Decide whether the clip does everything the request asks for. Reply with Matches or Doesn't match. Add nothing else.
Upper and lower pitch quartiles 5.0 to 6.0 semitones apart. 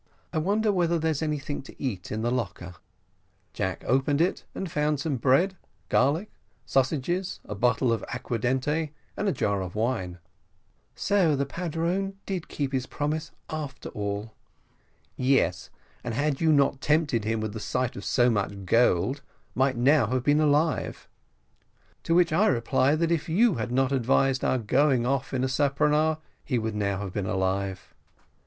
Matches